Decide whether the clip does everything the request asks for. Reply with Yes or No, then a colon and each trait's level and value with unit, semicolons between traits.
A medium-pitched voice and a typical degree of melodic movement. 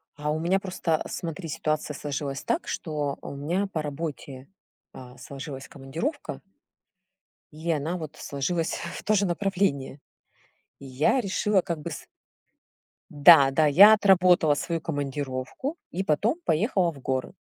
Yes: medium, 155 Hz; average, 4.4 semitones